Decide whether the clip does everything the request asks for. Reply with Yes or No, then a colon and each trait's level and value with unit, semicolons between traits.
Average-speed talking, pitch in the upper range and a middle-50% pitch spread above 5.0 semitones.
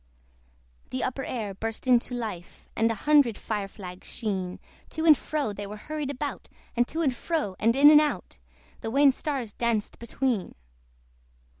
Yes: average, 165 wpm; high, 235 Hz; wide, 5.5 semitones